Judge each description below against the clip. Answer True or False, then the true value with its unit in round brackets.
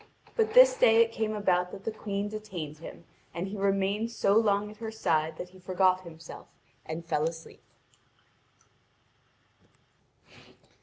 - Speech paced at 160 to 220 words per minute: False (145 wpm)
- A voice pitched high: True (195 Hz)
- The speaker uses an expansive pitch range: False (3.9 semitones)